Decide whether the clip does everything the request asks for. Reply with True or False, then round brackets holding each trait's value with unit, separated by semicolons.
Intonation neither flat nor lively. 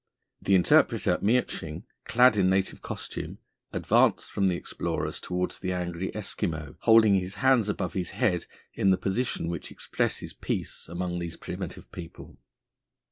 True (3.1 semitones)